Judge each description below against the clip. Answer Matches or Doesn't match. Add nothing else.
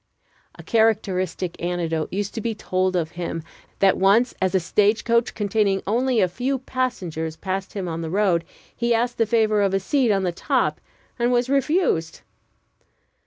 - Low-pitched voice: Doesn't match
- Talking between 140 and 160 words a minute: Doesn't match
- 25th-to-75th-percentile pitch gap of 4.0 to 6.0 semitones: Matches